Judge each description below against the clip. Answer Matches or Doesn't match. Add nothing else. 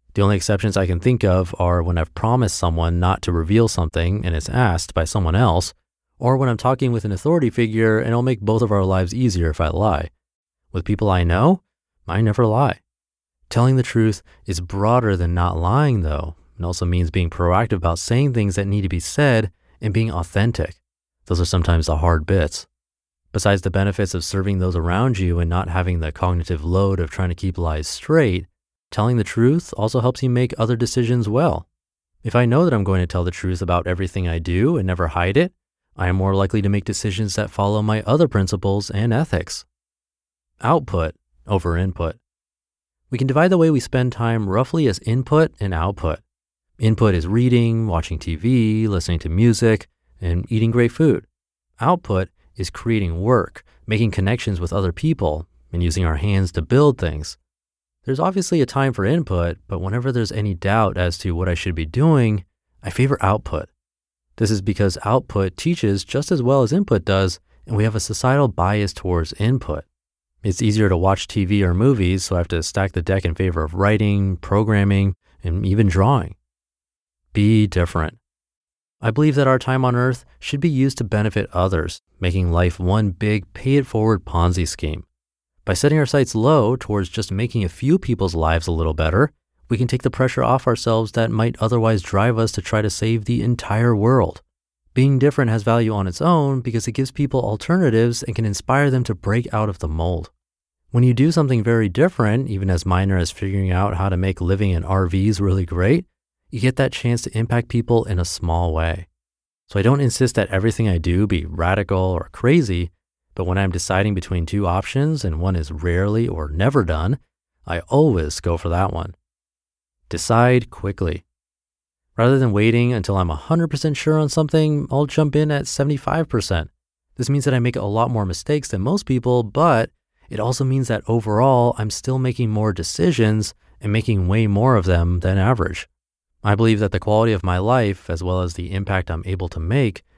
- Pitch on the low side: Matches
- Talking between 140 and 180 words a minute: Doesn't match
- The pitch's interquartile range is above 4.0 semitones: Matches